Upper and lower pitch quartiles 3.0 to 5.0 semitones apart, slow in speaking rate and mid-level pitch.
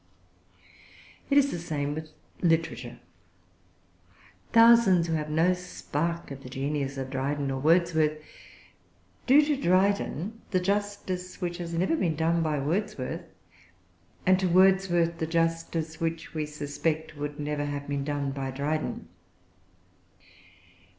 Yes: average, 3.8 semitones; slow, 130 wpm; medium, 165 Hz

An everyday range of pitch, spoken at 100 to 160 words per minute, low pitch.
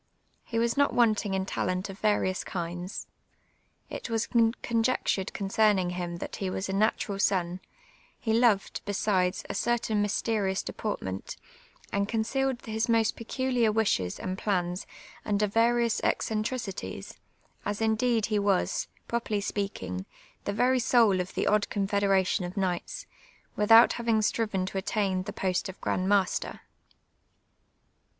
No: average, 3.1 semitones; slow, 135 wpm; high, 205 Hz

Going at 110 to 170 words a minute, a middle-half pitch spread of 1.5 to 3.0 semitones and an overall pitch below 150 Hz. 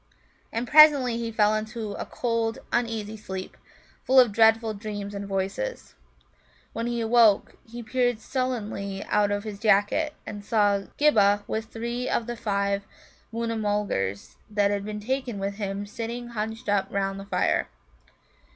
No: average, 150 wpm; narrow, 2.6 semitones; high, 215 Hz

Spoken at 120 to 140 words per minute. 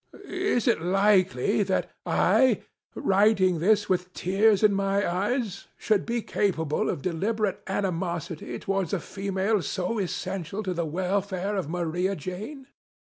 Yes: slow, 135 wpm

